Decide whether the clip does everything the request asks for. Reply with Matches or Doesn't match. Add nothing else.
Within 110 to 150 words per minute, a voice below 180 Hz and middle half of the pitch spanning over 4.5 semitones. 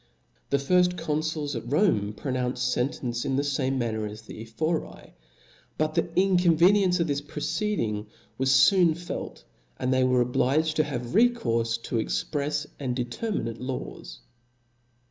Matches